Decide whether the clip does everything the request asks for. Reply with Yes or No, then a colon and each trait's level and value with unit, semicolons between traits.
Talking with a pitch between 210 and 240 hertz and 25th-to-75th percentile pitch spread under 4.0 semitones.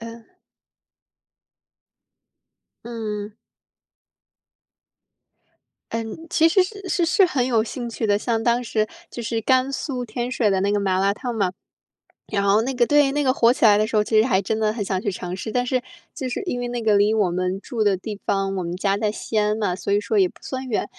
Yes: high, 220 Hz; average, 3.4 semitones